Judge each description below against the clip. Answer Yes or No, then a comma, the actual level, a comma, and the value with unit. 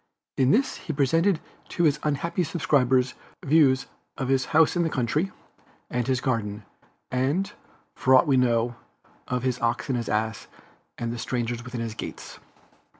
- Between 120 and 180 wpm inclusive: Yes, average, 160 wpm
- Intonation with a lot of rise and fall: No, average, 4.0 semitones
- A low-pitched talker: Yes, low, 130 Hz